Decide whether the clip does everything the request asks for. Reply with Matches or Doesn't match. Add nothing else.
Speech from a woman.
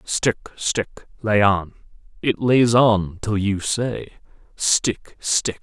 Doesn't match